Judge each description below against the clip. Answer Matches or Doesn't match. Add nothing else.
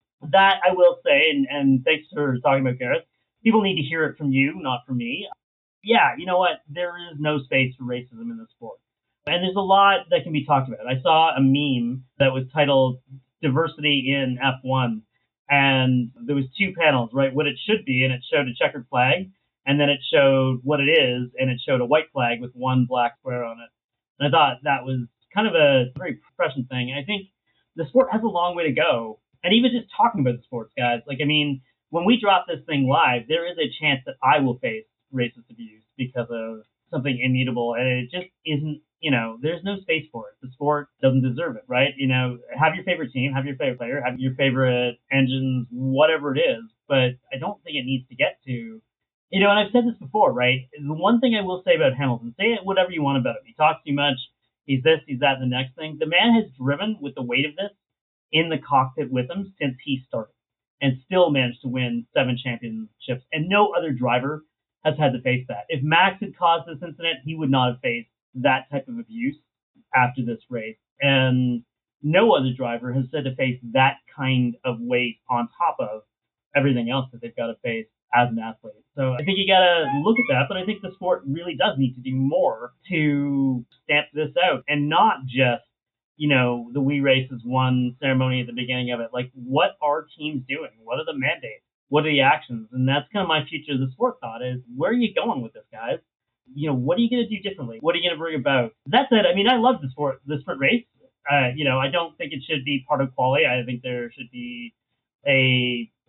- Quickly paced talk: Matches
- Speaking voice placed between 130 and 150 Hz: Matches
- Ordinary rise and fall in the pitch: Matches